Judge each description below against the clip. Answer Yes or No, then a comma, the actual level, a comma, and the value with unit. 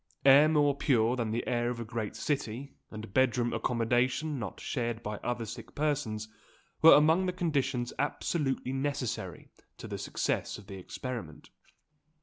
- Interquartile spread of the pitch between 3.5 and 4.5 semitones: Yes, average, 3.9 semitones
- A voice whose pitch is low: Yes, low, 125 Hz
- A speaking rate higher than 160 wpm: No, average, 155 wpm